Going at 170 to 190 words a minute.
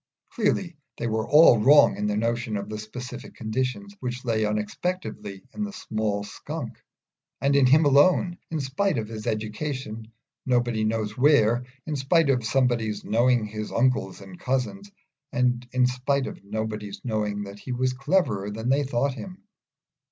No: average, 160 wpm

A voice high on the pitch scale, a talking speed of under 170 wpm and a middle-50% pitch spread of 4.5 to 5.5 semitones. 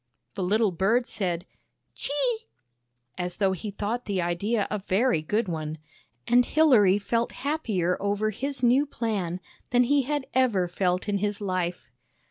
Yes: high, 205 Hz; average, 160 wpm; average, 5.0 semitones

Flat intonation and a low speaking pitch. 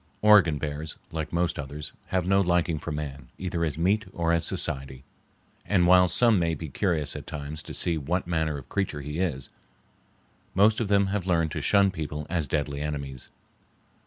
No: average, 3.7 semitones; very low, 80 Hz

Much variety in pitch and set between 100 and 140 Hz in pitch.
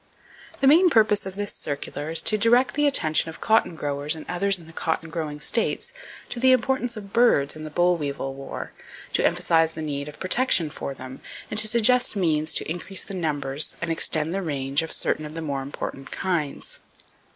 No: wide, 6.3 semitones; medium, 165 Hz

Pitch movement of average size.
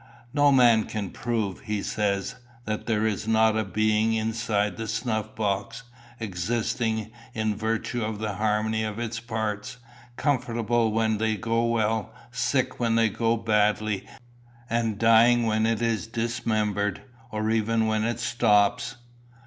No: narrow, 1.3 semitones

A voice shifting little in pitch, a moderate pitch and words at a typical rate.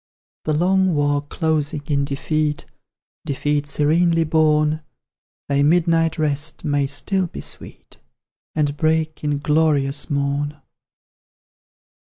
No: narrow, 1.9 semitones; medium, 150 Hz; slow, 105 wpm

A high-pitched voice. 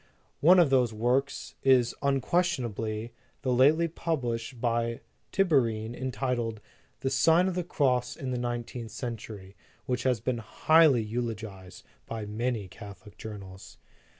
No: low, 120 Hz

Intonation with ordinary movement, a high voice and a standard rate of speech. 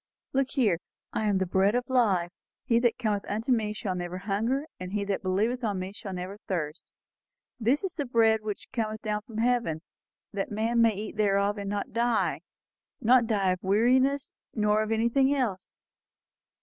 Yes: average, 3.2 semitones; high, 215 Hz; average, 185 wpm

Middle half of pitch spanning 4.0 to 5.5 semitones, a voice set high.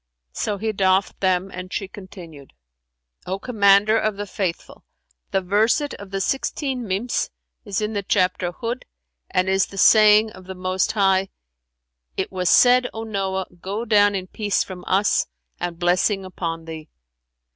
No: narrow, 2.4 semitones; high, 195 Hz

